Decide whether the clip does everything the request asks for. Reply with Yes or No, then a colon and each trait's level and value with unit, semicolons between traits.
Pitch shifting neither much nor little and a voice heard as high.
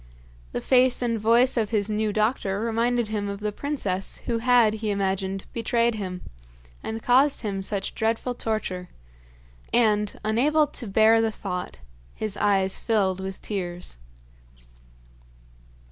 Yes: average, 3.0 semitones; high, 215 Hz